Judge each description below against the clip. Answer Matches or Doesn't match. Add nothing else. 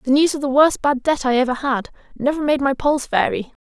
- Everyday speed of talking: Doesn't match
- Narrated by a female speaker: Matches